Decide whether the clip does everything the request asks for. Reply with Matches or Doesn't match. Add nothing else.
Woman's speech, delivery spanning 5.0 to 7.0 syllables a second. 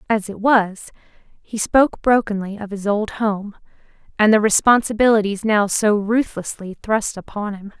Doesn't match